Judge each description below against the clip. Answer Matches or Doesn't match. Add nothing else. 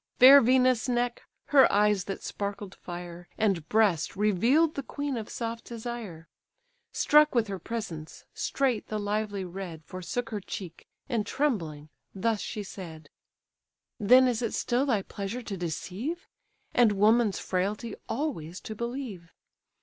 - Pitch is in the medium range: Doesn't match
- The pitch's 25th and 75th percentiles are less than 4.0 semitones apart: Doesn't match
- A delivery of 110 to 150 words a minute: Matches